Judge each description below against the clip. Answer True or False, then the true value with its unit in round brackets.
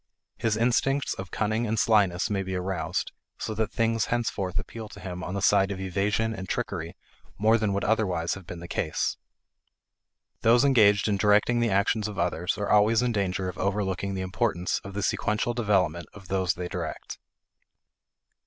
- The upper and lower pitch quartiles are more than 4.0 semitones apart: False (3.0 semitones)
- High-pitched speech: False (100 Hz)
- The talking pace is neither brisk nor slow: True (180 wpm)